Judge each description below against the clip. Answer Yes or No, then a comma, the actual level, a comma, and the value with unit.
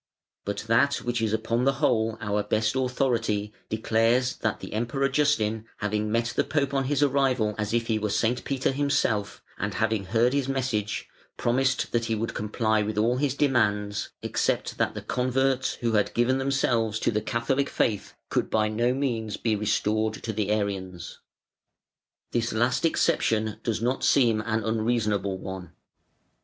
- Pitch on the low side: Yes, low, 115 Hz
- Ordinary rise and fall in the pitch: Yes, average, 3.1 semitones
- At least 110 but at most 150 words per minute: No, average, 165 wpm